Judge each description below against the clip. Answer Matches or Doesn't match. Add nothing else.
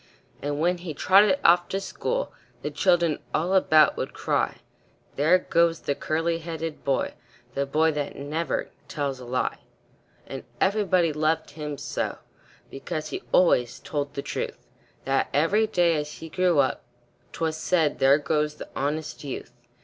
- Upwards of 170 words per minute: Doesn't match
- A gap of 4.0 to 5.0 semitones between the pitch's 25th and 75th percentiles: Doesn't match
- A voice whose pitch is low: Doesn't match